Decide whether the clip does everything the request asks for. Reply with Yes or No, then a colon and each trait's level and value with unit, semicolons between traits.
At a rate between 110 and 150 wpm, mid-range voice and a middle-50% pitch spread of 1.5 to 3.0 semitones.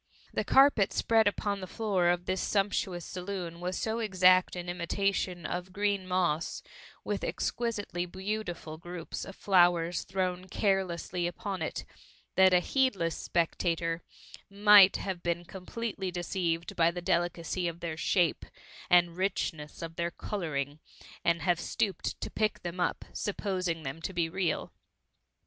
Yes: average, 140 wpm; medium, 180 Hz; narrow, 2.4 semitones